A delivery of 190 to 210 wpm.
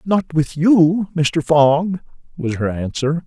No: average, 145 wpm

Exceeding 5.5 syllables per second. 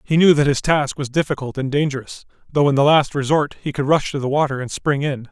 Yes: 6.0 syllables/s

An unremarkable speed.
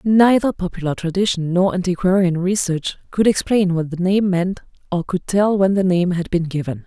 Yes: average, 185 wpm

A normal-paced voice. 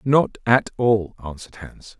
Yes: average, 150 wpm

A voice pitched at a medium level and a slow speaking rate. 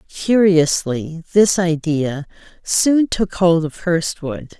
Yes: medium, 170 Hz; slow, 105 wpm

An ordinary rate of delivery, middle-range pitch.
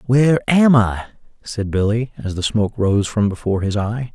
No: average, 190 wpm; low, 110 Hz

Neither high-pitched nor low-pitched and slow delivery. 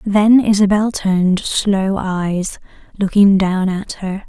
No: high, 195 Hz; slow, 125 wpm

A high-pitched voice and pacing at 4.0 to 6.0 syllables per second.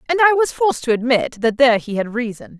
No: very high, 260 Hz; 6.3 syllables/s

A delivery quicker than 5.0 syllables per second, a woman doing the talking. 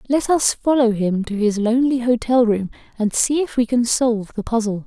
Yes: 5.2 syllables/s; female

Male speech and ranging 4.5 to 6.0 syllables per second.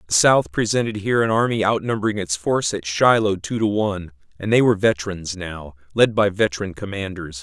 Yes: male; 5.9 syllables/s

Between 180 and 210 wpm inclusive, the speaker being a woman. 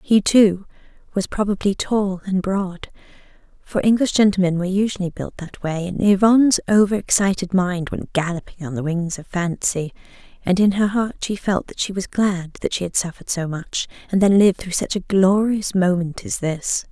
Yes: average, 185 wpm; female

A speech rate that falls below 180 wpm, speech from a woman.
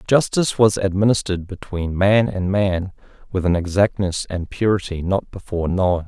No: average, 150 wpm; male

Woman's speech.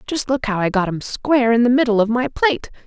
Yes: female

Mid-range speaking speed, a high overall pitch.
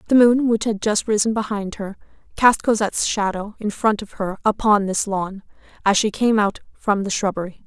Yes: average, 195 wpm; high, 210 Hz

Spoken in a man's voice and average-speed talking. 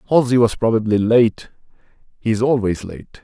No: male; slow, 130 wpm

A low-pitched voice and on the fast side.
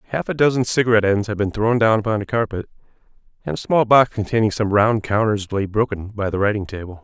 Yes: low, 105 Hz; fast, 220 wpm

